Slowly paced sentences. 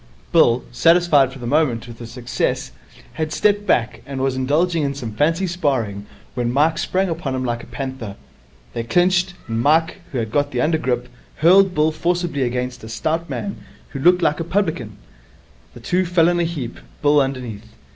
No: average, 185 wpm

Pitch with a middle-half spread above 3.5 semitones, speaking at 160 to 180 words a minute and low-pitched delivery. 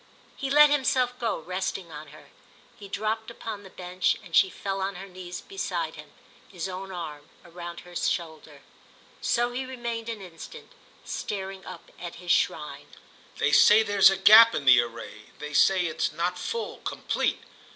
No: average, 4.6 semitones; average, 165 wpm; high, 190 Hz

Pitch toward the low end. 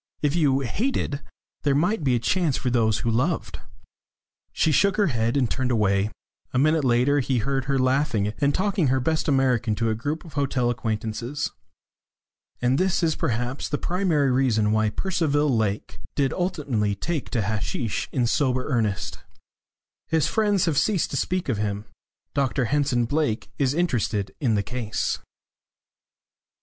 Yes: low, 130 Hz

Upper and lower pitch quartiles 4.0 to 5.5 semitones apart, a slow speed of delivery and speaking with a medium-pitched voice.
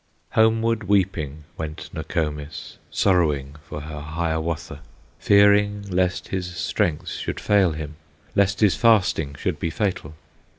No: average, 4.9 semitones; slow, 120 wpm; very low, 85 Hz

